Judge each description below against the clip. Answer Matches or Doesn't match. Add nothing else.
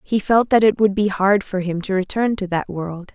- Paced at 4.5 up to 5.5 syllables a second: Matches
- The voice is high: Matches